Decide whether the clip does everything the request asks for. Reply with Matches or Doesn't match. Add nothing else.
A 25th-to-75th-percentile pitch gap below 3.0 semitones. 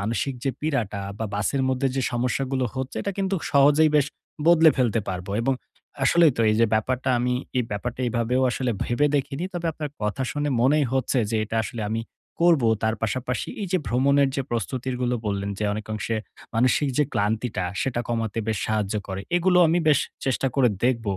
Doesn't match